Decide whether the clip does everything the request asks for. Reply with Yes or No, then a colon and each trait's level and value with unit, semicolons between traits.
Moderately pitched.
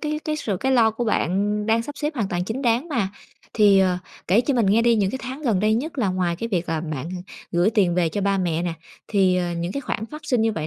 No: high, 210 Hz